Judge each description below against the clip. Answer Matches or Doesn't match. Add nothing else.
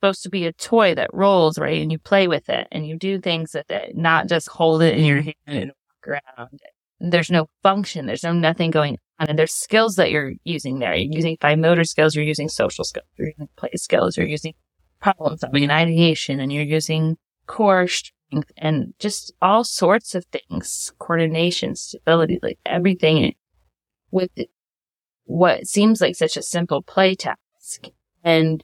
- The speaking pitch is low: Doesn't match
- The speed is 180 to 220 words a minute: Matches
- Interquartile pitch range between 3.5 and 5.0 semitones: Doesn't match